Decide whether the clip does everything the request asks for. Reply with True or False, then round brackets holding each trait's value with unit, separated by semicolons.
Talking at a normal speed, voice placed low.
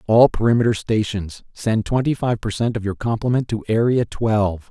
True (180 wpm; 110 Hz)